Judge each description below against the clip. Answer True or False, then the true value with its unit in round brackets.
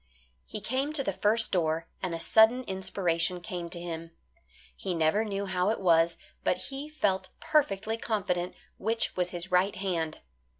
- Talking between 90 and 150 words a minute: False (165 wpm)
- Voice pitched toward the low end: False (190 Hz)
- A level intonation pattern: False (4.1 semitones)